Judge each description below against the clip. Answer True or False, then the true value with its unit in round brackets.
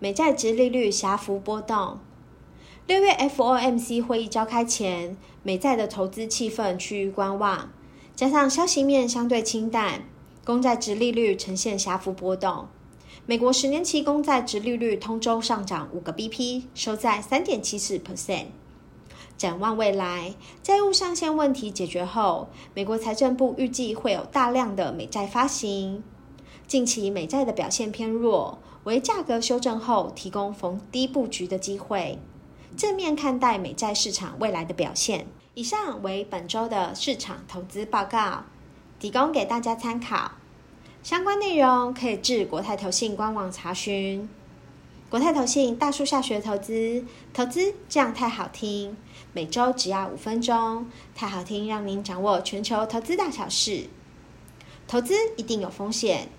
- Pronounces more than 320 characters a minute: False (240 characters per minute)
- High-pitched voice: True (225 Hz)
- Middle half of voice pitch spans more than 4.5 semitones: False (4.1 semitones)